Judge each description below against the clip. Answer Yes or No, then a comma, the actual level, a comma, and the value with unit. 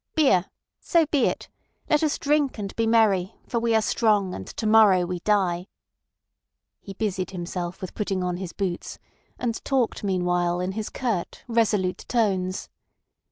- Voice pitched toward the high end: Yes, high, 200 Hz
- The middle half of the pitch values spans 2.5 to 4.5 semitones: Yes, average, 3.9 semitones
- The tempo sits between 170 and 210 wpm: No, average, 160 wpm